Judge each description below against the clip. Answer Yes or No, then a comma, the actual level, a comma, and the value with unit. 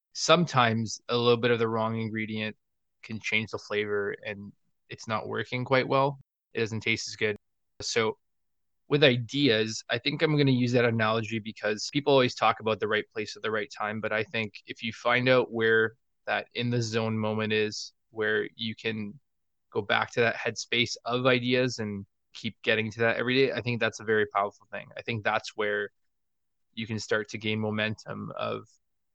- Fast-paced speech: No, average, 195 wpm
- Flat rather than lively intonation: Yes, narrow, 2.1 semitones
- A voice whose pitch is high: No, low, 110 Hz